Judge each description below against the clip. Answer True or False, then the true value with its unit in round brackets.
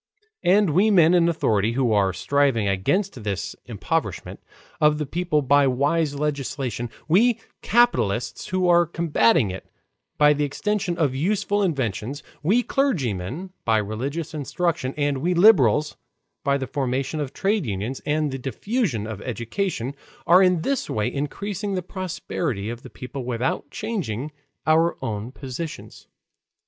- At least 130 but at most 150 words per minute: True (140 wpm)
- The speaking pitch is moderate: True (145 Hz)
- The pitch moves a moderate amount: False (6.4 semitones)